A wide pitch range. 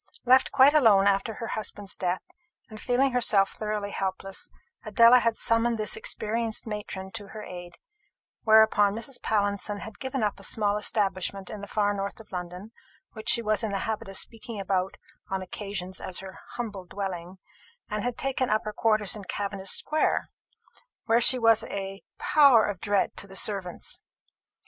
No: narrow, 2.6 semitones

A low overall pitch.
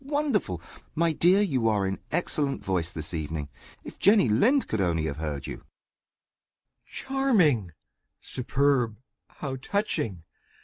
Yes: low, 125 Hz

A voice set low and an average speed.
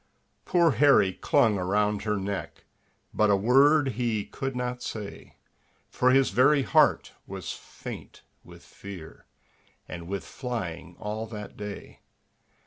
No: low, 110 Hz; slow, 130 wpm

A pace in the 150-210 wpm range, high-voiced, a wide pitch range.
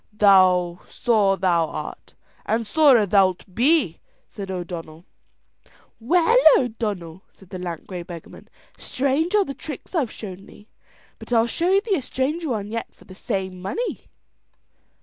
No: average, 140 wpm; high, 215 Hz; wide, 7.1 semitones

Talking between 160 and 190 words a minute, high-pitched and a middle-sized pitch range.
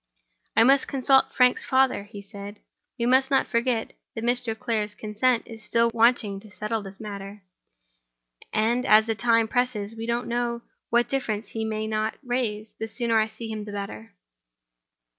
No: average, 170 wpm; high, 225 Hz; narrow, 2.2 semitones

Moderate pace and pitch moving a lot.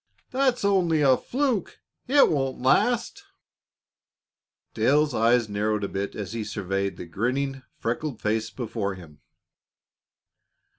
No: slow, 120 wpm; wide, 7.1 semitones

